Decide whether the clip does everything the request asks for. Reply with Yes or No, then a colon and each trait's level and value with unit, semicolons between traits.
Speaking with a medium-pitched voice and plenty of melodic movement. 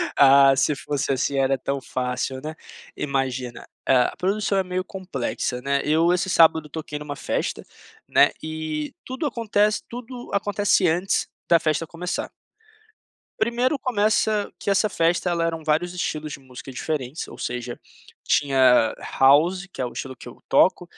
Yes: medium, 155 Hz; wide, 5.8 semitones